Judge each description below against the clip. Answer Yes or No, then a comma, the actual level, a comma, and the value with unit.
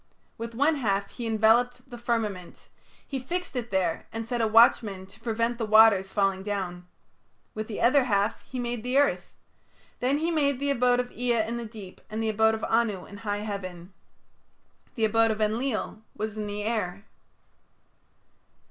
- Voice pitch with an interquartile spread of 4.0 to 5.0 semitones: No, average, 2.9 semitones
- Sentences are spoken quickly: No, average, 175 wpm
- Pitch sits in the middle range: No, high, 225 Hz